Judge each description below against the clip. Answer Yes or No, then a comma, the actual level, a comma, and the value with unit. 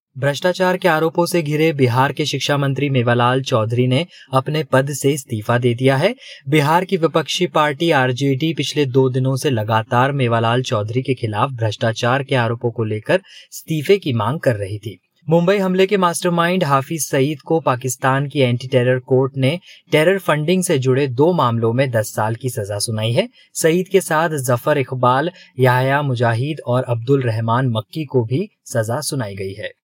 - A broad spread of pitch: No, average, 4.2 semitones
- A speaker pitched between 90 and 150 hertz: Yes, low, 135 Hz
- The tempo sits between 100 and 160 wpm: No, average, 175 wpm